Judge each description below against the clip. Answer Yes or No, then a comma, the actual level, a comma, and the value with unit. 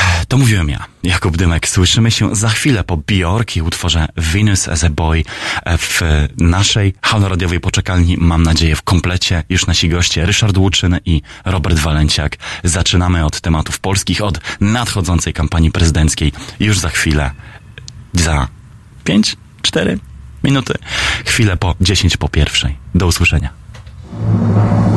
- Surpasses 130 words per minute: No, average, 125 wpm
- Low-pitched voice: Yes, very low, 90 Hz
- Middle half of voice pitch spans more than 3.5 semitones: Yes, average, 4.1 semitones